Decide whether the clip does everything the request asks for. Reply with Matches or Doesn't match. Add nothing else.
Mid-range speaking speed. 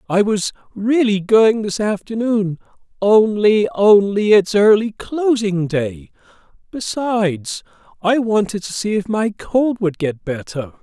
Doesn't match